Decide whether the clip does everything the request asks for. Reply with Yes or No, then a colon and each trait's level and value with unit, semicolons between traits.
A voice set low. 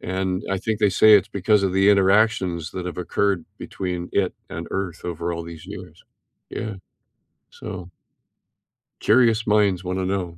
Yes: very low, 95 Hz